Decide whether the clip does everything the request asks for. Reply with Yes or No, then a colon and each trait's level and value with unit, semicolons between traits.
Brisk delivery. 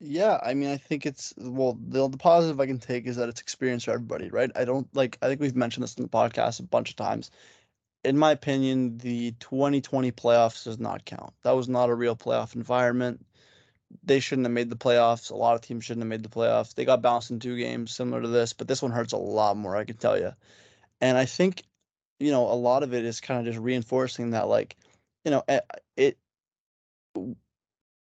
Yes: fast, 225 wpm